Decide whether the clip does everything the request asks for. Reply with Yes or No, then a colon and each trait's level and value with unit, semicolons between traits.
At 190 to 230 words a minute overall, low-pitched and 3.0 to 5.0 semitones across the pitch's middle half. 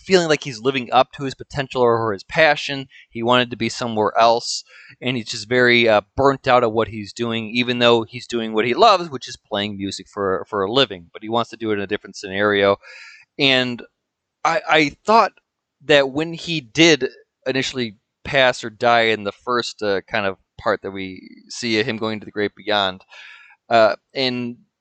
Yes: fast, 205 wpm; low, 120 Hz; average, 3.6 semitones